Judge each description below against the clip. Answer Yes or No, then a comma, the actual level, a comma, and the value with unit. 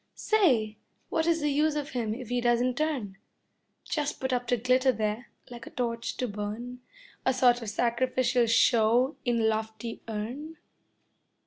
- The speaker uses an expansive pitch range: No, average, 2.7 semitones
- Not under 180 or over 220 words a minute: No, average, 160 wpm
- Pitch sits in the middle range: No, high, 245 Hz